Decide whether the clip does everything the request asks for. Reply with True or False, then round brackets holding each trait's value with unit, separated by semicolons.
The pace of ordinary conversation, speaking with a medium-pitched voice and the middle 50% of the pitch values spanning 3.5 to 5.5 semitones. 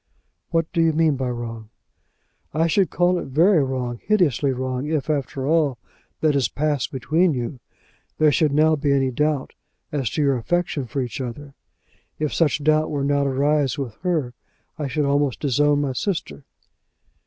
False (175 wpm; 145 Hz; 3.0 semitones)